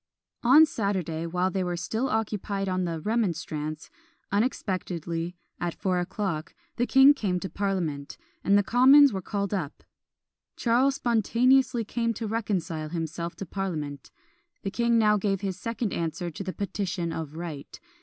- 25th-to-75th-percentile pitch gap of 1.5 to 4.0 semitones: No, average, 4.8 semitones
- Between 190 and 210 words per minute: No, average, 150 wpm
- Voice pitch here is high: Yes, high, 195 Hz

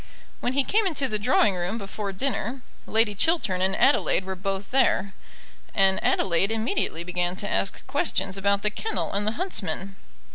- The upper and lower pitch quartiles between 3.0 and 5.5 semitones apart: Yes, average, 3.8 semitones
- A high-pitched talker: Yes, high, 200 Hz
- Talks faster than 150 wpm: Yes, average, 170 wpm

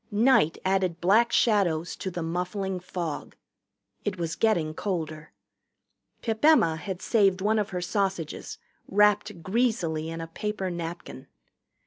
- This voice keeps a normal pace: No, slow, 130 wpm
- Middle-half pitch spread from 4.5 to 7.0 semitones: No, average, 4.0 semitones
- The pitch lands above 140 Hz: Yes, medium, 185 Hz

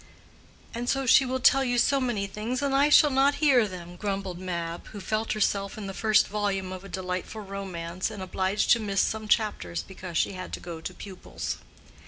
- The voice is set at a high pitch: Yes, high, 200 Hz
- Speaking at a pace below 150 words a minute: No, average, 200 wpm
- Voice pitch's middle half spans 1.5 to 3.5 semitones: No, average, 4.0 semitones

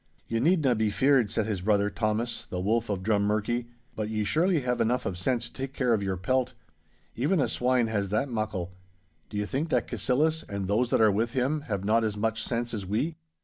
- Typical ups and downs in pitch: Yes, average, 3.6 semitones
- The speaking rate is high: Yes, fast, 220 wpm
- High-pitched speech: No, low, 115 Hz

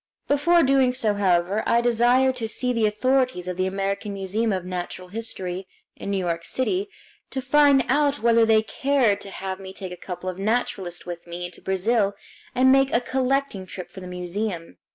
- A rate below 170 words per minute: No, average, 190 wpm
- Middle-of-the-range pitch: No, high, 210 Hz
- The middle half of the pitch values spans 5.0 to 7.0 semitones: Yes, wide, 5.4 semitones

